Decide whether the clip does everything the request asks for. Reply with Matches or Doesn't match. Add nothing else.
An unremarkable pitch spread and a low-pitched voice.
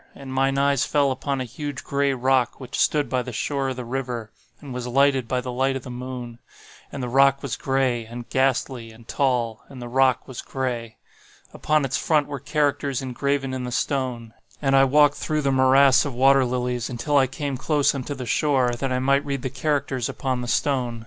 Doesn't match